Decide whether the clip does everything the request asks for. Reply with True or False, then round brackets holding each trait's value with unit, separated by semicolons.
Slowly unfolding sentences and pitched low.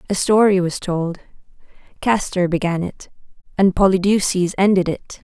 False (125 wpm; 185 Hz)